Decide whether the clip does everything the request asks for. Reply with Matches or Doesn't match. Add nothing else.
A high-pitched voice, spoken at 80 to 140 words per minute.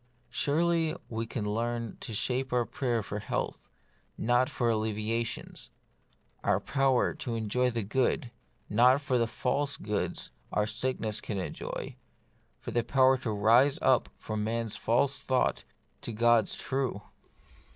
Doesn't match